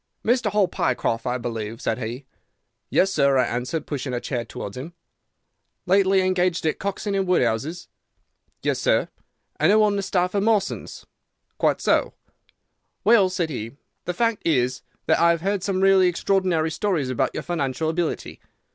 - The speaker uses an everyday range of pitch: No, wide, 7.1 semitones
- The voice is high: No, medium, 170 Hz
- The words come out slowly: No, average, 165 wpm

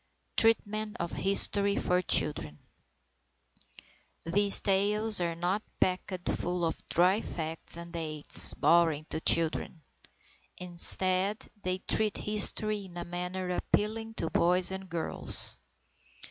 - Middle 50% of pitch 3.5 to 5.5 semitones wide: No, average, 3.1 semitones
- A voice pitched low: No, medium, 185 Hz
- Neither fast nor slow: No, slow, 115 wpm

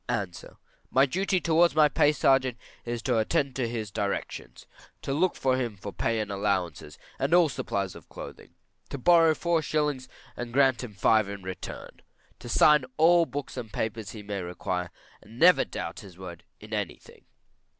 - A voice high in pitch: No, low, 120 Hz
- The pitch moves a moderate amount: No, wide, 6.7 semitones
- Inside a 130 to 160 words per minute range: No, average, 180 wpm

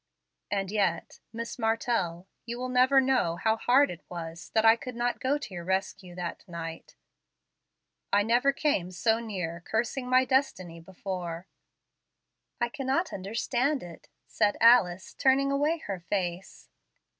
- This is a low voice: No, high, 220 Hz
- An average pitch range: No, wide, 6.1 semitones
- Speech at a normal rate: Yes, average, 145 wpm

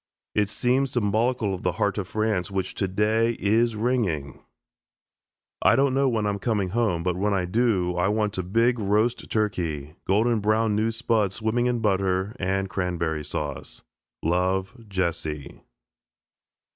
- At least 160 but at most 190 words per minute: No, average, 145 wpm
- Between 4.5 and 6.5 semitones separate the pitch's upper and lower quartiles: No, average, 3.7 semitones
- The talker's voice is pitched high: No, low, 105 Hz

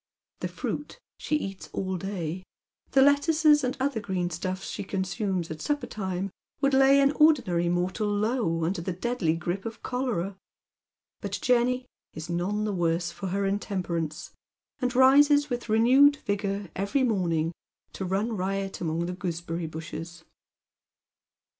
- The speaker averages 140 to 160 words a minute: Yes, average, 145 wpm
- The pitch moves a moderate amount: No, wide, 6.2 semitones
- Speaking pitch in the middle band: No, high, 195 Hz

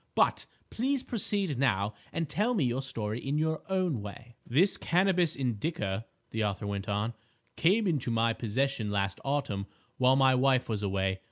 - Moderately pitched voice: No, low, 130 Hz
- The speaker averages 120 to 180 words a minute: Yes, average, 165 wpm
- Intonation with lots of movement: Yes, wide, 7.6 semitones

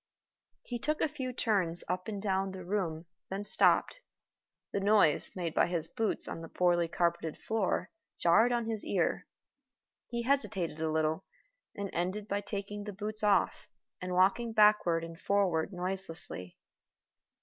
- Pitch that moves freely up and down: No, average, 3.7 semitones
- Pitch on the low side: No, high, 195 Hz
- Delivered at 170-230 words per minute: No, average, 150 wpm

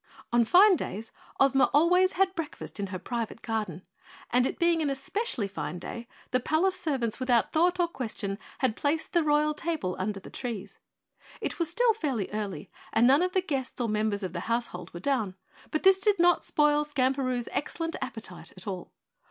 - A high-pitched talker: Yes, very high, 265 Hz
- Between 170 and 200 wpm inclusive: Yes, average, 185 wpm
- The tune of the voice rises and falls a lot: Yes, wide, 7.5 semitones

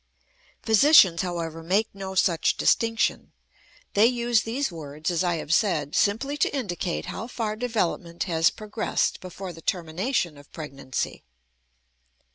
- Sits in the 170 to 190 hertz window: Yes, medium, 185 Hz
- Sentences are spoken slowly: Yes, slow, 130 wpm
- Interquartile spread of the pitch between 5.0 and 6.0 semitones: Yes, wide, 5.4 semitones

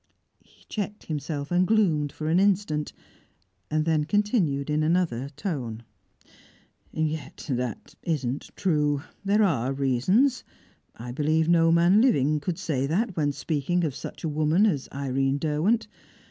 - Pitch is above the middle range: No, medium, 155 Hz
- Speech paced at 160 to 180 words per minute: No, slow, 135 wpm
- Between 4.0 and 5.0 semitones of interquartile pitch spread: Yes, average, 4.6 semitones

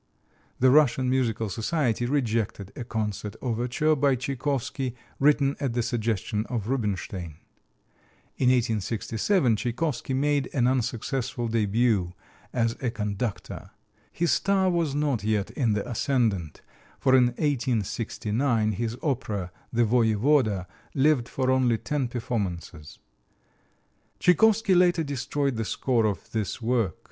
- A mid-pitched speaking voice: No, low, 120 Hz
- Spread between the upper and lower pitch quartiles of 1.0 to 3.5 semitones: No, average, 3.9 semitones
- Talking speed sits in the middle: No, slow, 120 wpm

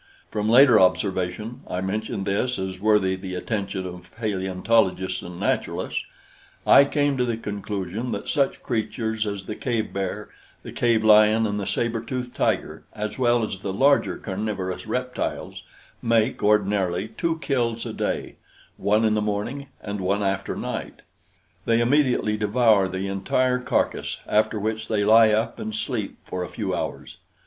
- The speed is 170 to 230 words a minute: No, average, 155 wpm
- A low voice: Yes, low, 105 Hz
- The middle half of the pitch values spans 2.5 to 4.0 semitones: Yes, average, 3.2 semitones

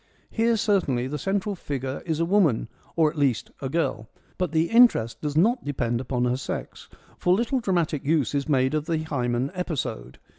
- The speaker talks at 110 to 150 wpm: No, average, 185 wpm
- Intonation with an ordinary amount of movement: No, wide, 5.8 semitones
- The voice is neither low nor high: Yes, medium, 150 Hz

